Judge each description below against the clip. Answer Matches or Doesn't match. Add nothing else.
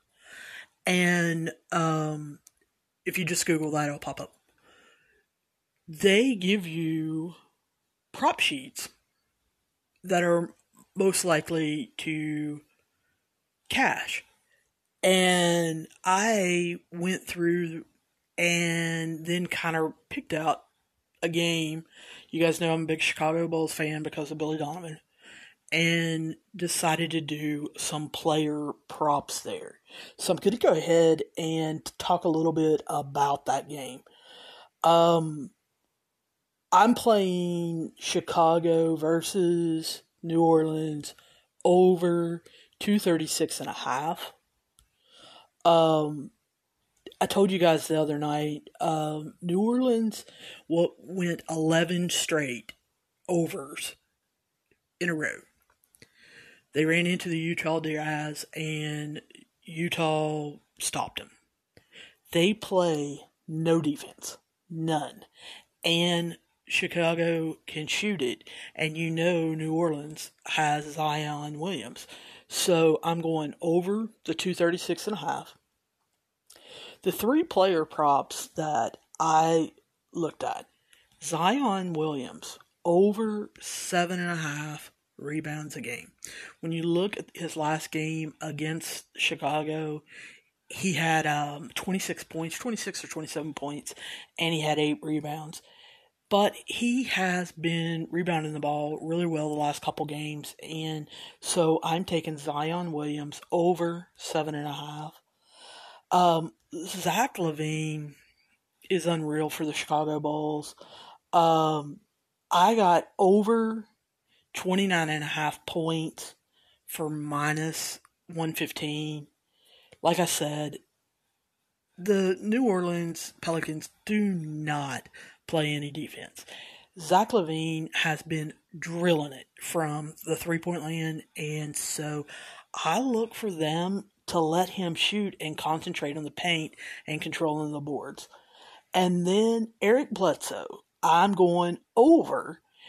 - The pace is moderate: Doesn't match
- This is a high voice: Doesn't match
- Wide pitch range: Doesn't match